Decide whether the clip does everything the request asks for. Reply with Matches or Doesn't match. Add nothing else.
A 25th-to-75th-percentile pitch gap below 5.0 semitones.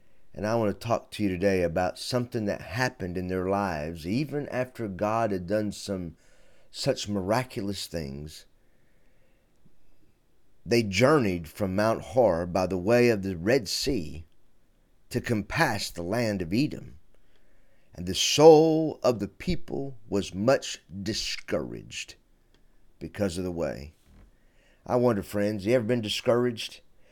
Matches